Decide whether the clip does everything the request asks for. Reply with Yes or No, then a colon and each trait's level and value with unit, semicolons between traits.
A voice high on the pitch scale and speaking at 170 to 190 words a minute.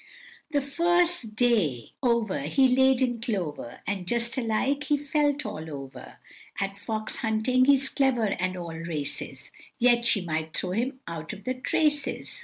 No: high, 235 Hz; average, 155 wpm